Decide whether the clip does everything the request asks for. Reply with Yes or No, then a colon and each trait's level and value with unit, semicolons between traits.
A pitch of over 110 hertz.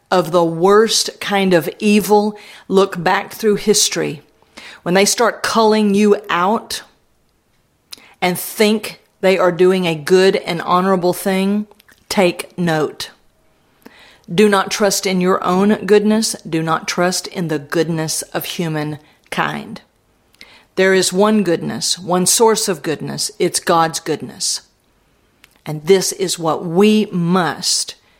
Yes: high, 190 Hz